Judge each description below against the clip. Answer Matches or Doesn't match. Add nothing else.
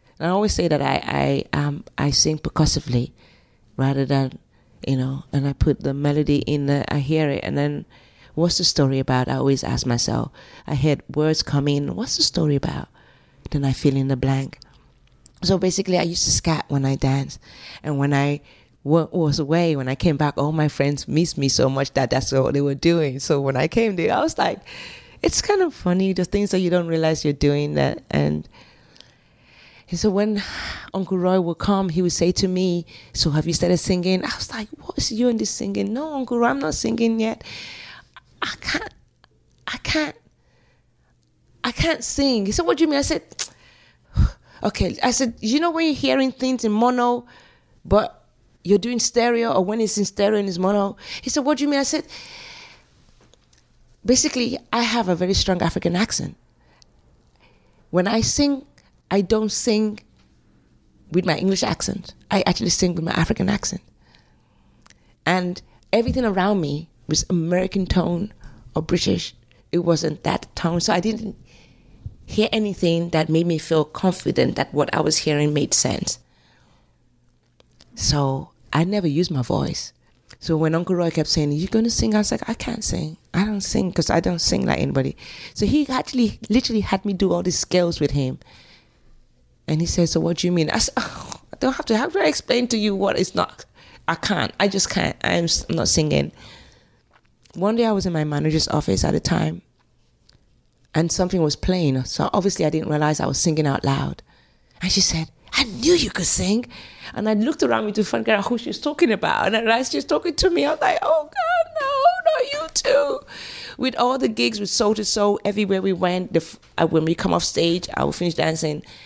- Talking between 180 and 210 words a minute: Matches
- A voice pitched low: Doesn't match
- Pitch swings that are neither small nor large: Doesn't match